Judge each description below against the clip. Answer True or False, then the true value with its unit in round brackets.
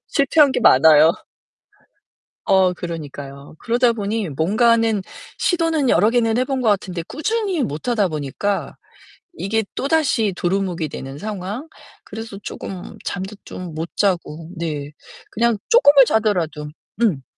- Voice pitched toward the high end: True (200 Hz)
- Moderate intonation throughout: False (6.3 semitones)